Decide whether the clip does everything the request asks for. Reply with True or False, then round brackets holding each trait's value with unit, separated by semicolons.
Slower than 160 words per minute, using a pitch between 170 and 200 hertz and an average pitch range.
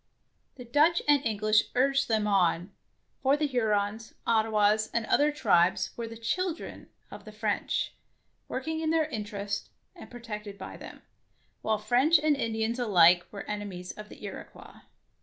False (150 wpm; 220 Hz; 4.4 semitones)